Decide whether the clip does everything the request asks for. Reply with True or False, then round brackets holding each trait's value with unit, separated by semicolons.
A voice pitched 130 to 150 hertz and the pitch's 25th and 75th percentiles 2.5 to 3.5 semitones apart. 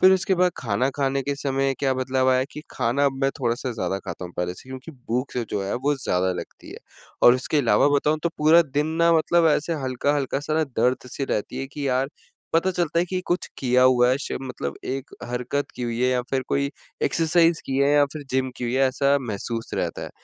True (135 Hz; 2.8 semitones)